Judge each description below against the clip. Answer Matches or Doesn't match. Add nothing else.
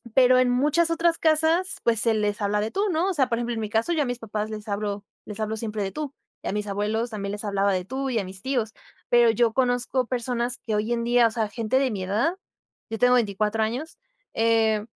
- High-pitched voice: Matches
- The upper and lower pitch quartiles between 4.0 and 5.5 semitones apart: Doesn't match